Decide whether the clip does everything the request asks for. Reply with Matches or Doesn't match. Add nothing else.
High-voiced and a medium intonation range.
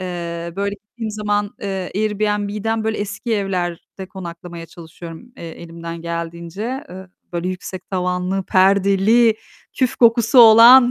Matches